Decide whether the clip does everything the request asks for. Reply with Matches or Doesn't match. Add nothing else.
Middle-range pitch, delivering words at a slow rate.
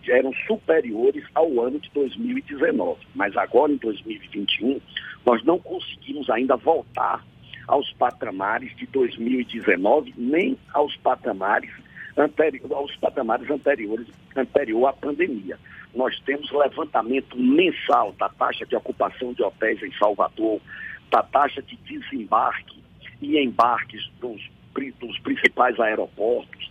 Matches